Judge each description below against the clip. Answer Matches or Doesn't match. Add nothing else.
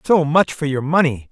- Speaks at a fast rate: Matches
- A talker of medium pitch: Matches